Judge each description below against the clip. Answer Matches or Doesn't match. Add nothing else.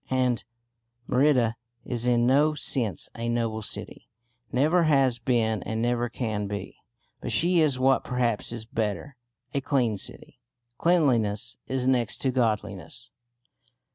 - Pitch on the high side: Doesn't match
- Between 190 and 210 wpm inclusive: Doesn't match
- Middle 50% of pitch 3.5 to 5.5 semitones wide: Doesn't match